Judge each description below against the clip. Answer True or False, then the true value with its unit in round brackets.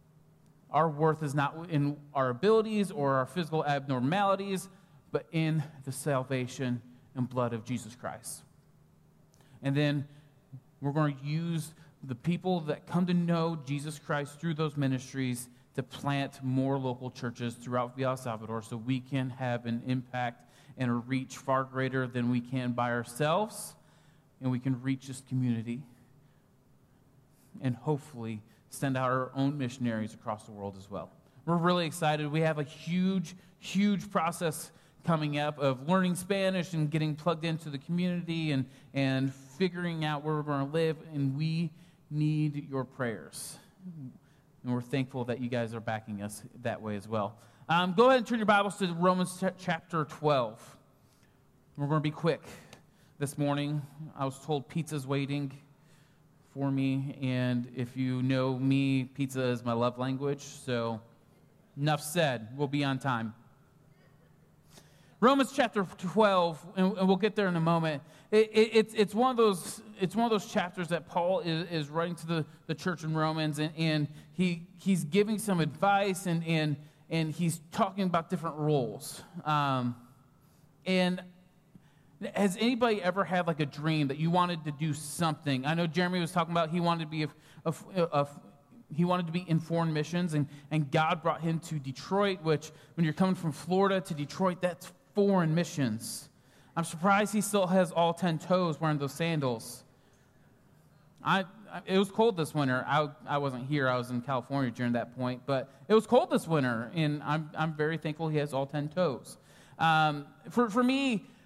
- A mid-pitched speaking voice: True (150 Hz)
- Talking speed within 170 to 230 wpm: True (175 wpm)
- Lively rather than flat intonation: False (4.6 semitones)